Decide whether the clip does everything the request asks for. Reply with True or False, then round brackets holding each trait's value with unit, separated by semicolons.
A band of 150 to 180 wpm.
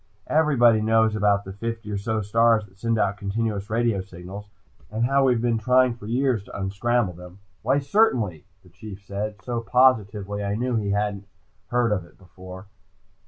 True (175 wpm)